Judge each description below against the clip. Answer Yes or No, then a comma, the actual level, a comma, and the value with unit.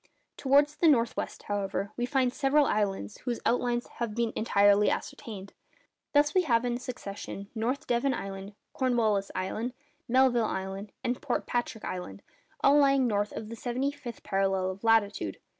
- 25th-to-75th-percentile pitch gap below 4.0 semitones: No, average, 4.4 semitones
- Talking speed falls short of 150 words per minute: No, average, 160 wpm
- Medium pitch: No, high, 235 Hz